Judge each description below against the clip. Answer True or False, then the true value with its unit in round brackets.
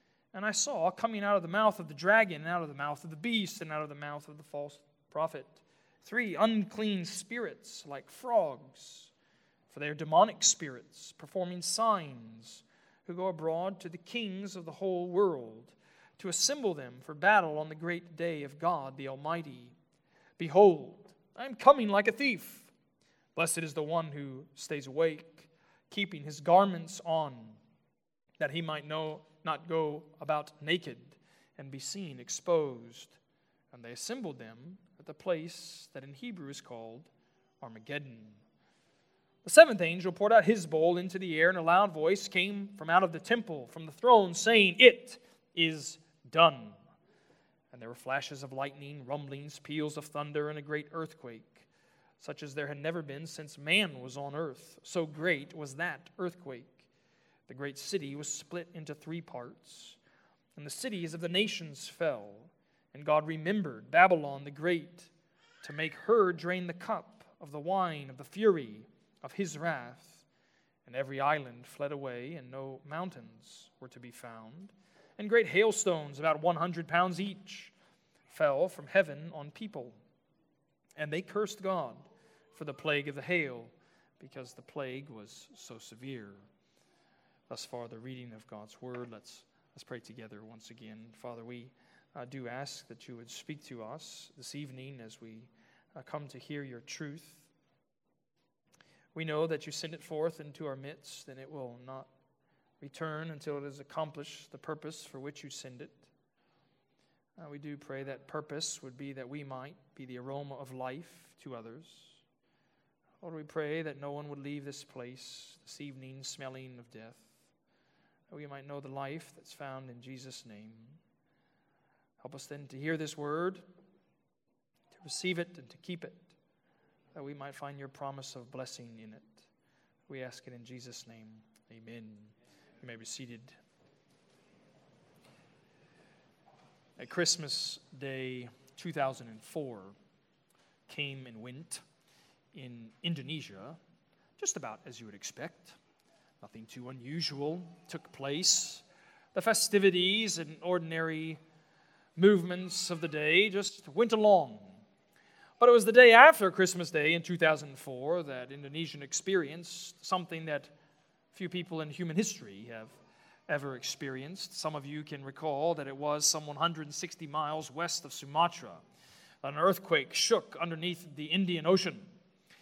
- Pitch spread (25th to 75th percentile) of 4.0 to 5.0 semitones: True (4.5 semitones)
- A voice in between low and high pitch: True (155 Hz)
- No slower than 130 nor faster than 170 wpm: True (160 wpm)